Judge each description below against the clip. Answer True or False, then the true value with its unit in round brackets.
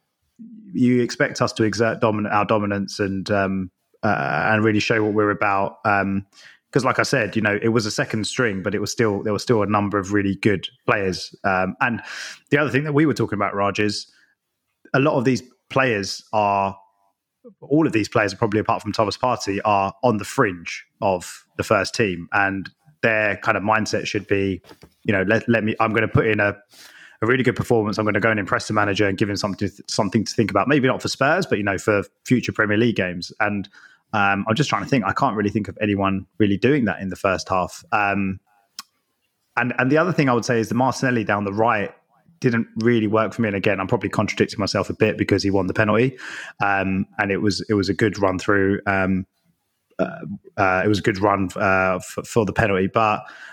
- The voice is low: True (105 Hz)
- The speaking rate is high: True (230 wpm)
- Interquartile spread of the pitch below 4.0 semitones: True (2.7 semitones)